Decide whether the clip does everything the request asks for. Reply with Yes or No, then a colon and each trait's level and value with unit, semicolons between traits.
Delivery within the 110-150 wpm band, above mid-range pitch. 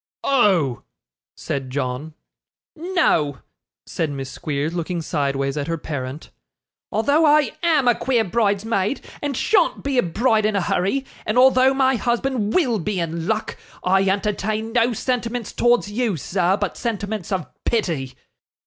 Yes: average, 145 wpm; high, 210 Hz